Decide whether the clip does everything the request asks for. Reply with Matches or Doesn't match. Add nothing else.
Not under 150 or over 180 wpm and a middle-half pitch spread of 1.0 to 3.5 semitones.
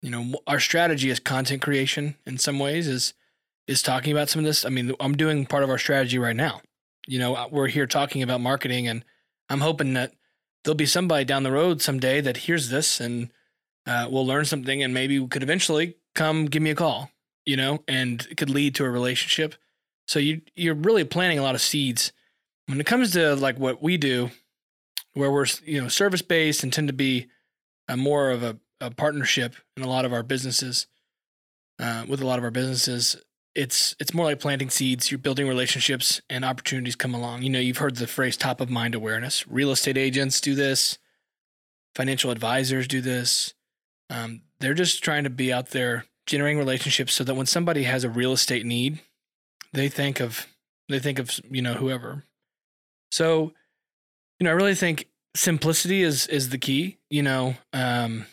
Doesn't match